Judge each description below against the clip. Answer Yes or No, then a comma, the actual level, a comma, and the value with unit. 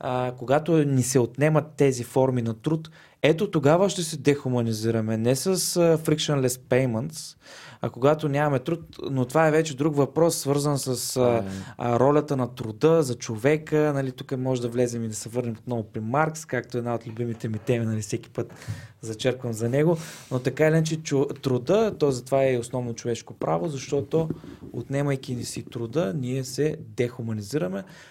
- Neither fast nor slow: No, fast, 175 wpm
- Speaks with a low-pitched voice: Yes, low, 130 Hz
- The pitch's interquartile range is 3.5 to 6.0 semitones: Yes, average, 4.1 semitones